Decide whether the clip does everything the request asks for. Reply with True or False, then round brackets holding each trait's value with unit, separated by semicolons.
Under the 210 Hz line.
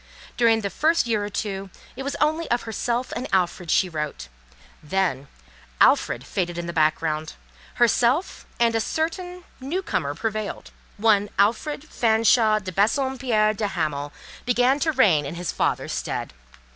False (215 Hz)